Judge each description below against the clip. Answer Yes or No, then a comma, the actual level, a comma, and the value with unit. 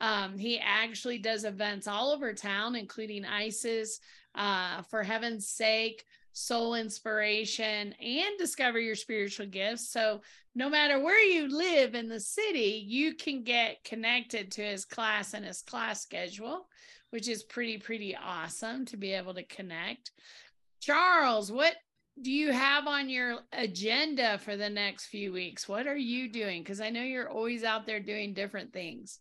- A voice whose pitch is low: No, high, 225 Hz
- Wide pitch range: No, average, 3.2 semitones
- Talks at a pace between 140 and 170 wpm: Yes, average, 160 wpm